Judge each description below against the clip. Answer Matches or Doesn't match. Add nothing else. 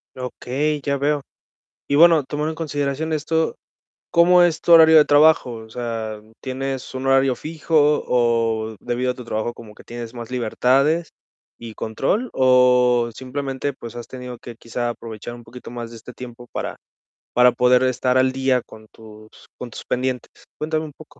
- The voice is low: Matches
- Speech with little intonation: Doesn't match